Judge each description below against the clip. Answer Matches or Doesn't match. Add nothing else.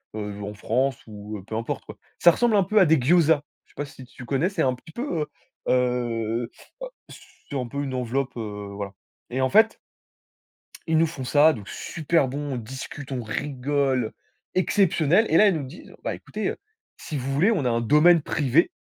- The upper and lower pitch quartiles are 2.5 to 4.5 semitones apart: Doesn't match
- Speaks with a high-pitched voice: Doesn't match